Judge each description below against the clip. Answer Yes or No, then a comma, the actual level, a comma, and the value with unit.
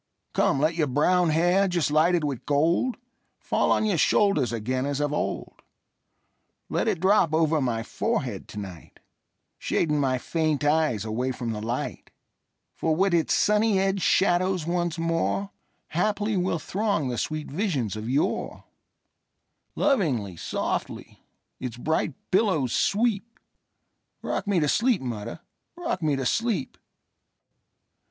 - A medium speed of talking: No, slow, 120 wpm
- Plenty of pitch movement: Yes, wide, 6.5 semitones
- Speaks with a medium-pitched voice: Yes, medium, 160 Hz